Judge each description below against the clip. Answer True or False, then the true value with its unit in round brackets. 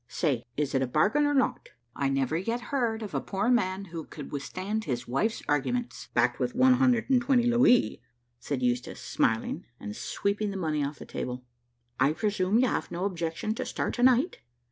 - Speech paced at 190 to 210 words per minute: True (195 wpm)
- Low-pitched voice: False (195 Hz)